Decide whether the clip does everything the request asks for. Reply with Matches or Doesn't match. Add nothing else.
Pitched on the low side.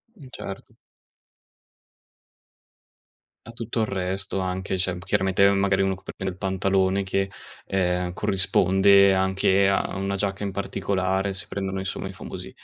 Matches